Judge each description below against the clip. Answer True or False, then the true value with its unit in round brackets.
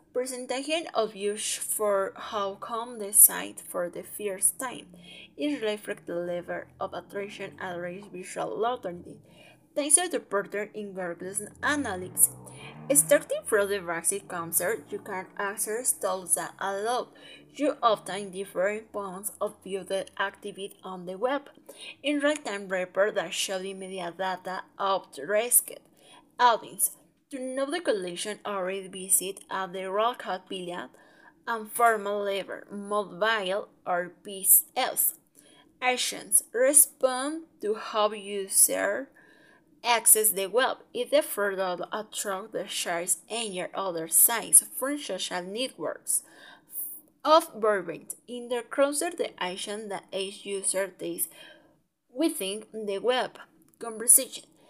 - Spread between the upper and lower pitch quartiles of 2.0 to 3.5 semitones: False (4.6 semitones)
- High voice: True (200 Hz)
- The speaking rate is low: True (125 wpm)